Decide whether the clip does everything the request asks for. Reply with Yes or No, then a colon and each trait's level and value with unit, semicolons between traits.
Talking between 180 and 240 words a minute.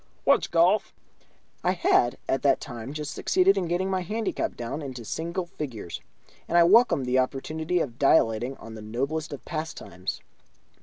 No: average, 160 wpm